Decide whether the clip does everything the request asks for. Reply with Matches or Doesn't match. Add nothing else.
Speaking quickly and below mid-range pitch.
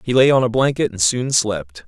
Matches